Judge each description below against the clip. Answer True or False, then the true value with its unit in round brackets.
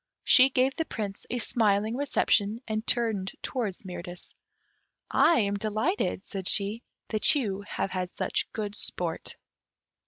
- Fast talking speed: False (135 wpm)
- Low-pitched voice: False (215 Hz)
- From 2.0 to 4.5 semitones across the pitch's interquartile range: True (3.3 semitones)